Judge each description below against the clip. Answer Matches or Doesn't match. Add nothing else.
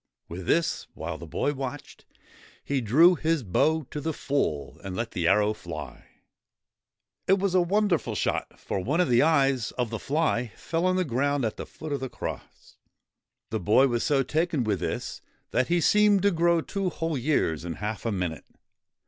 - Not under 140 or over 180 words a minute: Doesn't match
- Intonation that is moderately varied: Doesn't match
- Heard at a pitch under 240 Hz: Matches